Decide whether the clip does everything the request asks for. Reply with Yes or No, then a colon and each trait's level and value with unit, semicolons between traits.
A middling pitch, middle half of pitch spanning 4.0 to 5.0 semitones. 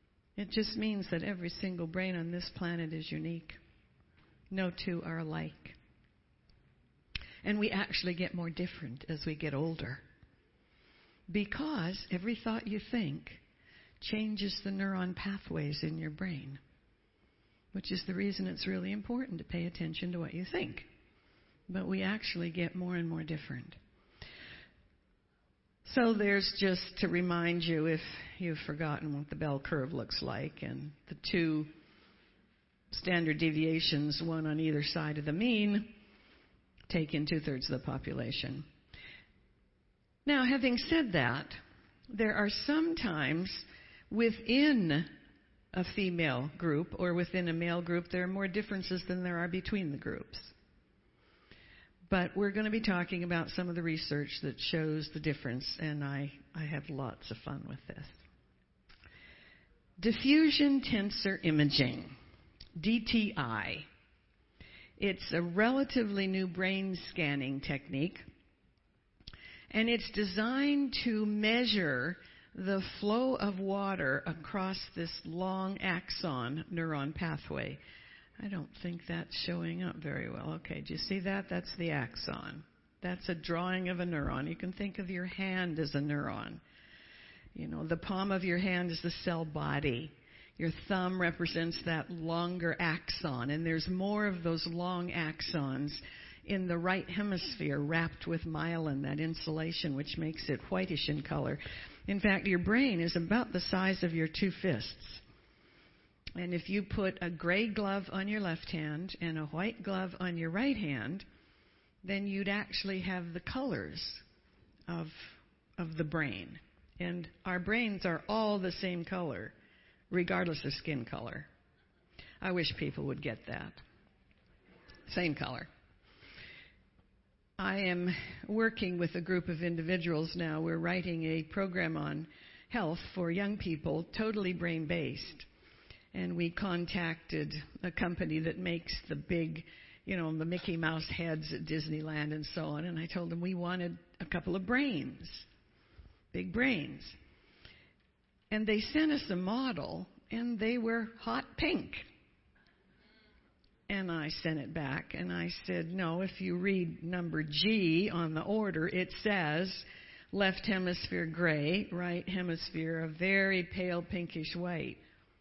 No: medium, 175 Hz; average, 3.4 semitones